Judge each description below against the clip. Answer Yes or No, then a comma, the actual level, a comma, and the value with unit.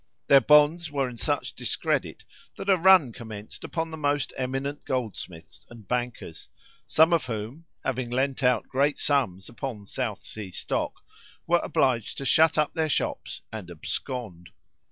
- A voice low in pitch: Yes, low, 130 Hz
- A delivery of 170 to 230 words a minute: No, average, 155 wpm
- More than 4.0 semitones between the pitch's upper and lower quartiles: Yes, average, 4.8 semitones